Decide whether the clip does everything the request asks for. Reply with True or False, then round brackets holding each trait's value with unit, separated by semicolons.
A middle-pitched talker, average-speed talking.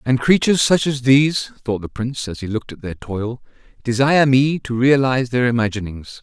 False (125 Hz; 195 wpm)